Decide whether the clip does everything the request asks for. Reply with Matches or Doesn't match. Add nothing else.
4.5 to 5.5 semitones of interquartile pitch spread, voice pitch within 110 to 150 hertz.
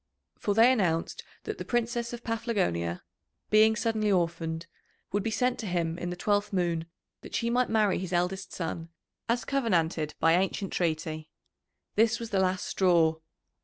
Doesn't match